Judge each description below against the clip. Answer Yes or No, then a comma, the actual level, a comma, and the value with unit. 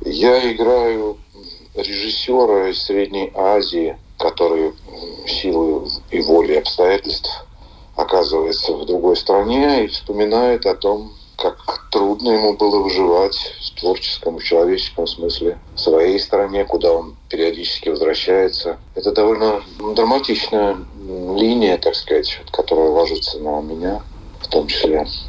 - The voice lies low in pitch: No, very high, 385 Hz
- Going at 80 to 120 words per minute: Yes, average, 115 wpm